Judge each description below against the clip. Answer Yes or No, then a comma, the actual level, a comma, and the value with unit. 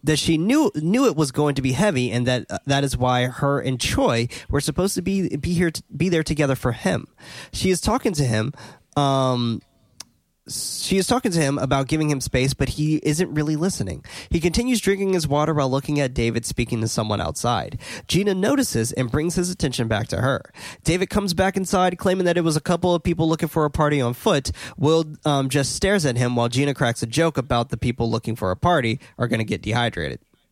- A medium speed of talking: No, fast, 225 wpm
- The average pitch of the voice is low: No, medium, 145 Hz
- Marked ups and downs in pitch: Yes, wide, 5.8 semitones